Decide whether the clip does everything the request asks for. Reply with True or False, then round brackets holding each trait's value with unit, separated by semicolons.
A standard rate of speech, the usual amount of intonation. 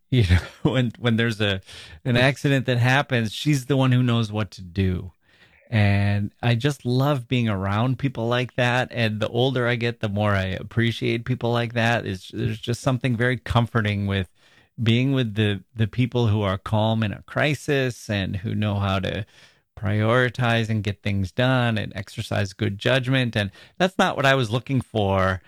True (185 wpm; 3.6 semitones)